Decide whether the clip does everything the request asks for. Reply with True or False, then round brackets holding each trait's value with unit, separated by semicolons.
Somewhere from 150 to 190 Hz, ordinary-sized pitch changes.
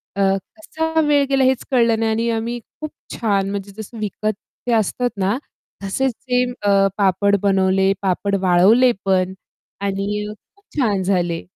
False (210 Hz; 4.0 semitones)